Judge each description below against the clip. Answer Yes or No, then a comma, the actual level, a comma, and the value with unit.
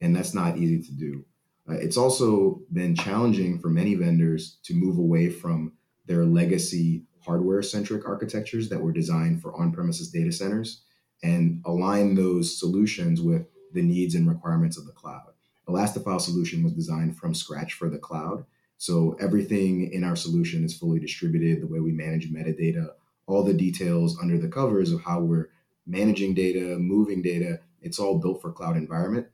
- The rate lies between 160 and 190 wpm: Yes, average, 170 wpm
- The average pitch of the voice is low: Yes, low, 100 Hz